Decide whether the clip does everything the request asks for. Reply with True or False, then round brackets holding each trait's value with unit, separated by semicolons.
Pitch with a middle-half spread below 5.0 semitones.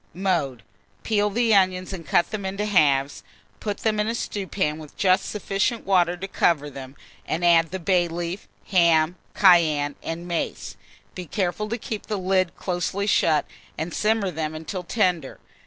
True (3.5 semitones)